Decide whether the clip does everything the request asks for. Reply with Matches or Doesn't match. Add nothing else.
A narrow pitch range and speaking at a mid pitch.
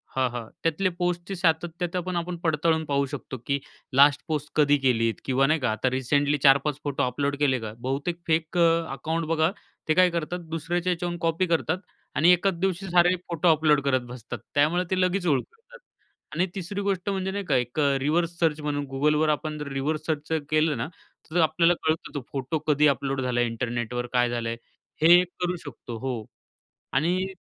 Doesn't match